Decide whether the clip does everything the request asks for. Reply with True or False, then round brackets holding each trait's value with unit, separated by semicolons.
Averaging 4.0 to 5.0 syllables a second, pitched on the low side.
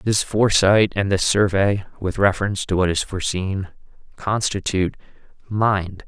True (4.8 syllables/s; 100 Hz)